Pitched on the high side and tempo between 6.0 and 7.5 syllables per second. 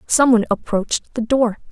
Yes: high, 230 Hz; 6.1 syllables/s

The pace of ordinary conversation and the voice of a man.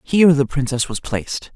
Yes: average, 195 wpm; male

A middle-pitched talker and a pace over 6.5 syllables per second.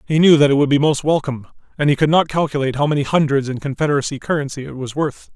Yes: medium, 145 Hz; 7.2 syllables/s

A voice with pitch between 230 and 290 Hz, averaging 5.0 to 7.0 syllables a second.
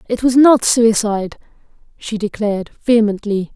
No: high, 220 Hz; 5.2 syllables/s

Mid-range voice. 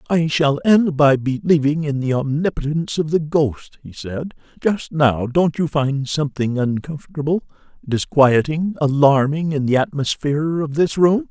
Yes: medium, 150 Hz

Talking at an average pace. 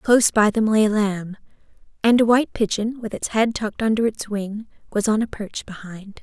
No: fast, 210 wpm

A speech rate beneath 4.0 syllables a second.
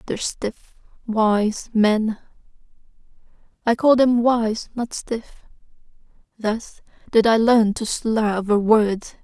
Yes: 3.2 syllables/s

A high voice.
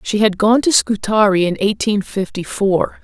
Yes: high, 205 Hz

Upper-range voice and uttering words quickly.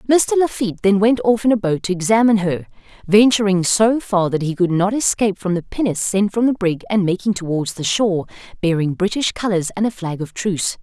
Yes: high, 200 Hz; fast, 215 wpm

